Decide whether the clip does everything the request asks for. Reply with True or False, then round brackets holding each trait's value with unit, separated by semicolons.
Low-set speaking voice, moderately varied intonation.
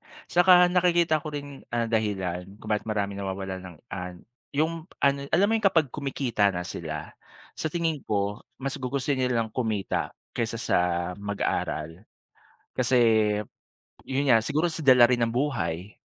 False (120 Hz; 6.7 semitones)